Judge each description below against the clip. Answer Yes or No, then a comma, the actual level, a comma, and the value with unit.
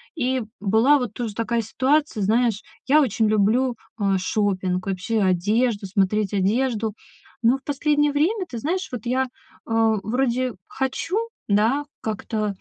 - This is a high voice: Yes, high, 230 Hz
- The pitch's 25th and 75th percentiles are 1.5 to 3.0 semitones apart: No, average, 4.2 semitones